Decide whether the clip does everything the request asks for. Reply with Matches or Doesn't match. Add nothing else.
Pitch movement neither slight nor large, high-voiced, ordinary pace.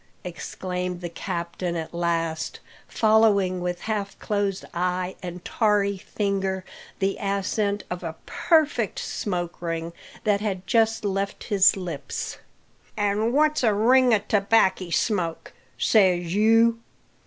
Doesn't match